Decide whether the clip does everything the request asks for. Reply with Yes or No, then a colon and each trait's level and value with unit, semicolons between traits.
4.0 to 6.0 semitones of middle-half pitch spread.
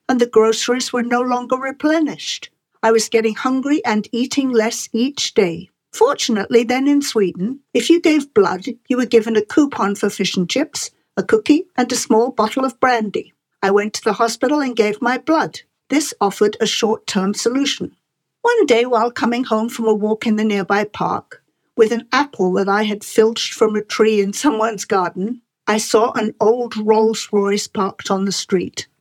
No: average, 3.4 semitones